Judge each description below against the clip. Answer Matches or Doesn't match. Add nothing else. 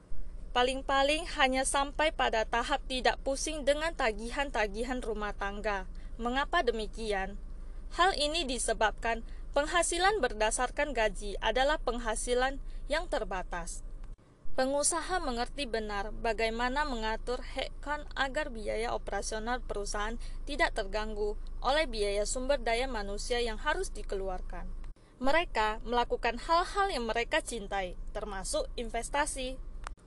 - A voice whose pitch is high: Matches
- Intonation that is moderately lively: Matches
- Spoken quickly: Doesn't match